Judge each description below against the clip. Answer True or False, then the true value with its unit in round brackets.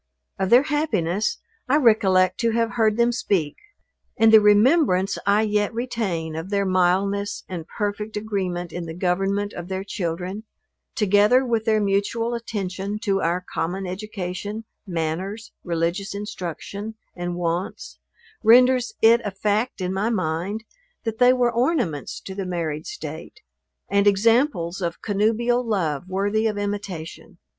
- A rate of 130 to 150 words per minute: True (140 wpm)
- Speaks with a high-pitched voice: True (200 Hz)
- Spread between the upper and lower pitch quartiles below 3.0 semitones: False (3.6 semitones)